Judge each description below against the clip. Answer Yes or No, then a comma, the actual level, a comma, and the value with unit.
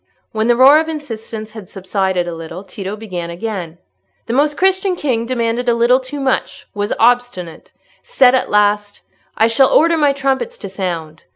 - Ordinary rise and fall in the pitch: No, wide, 5.7 semitones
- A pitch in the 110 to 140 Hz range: No, high, 230 Hz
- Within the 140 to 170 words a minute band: Yes, average, 165 wpm